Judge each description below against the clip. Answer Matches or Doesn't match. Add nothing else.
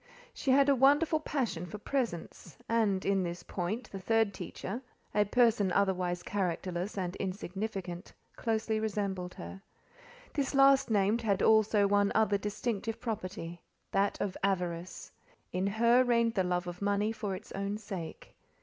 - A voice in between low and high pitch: Doesn't match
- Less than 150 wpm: Matches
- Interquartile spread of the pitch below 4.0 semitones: Matches